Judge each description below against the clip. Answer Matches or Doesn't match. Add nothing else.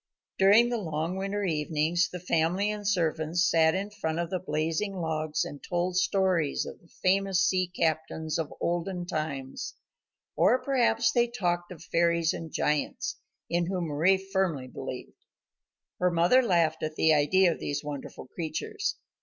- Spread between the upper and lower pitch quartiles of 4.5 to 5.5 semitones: Doesn't match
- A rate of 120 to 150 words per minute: Doesn't match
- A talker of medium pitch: Matches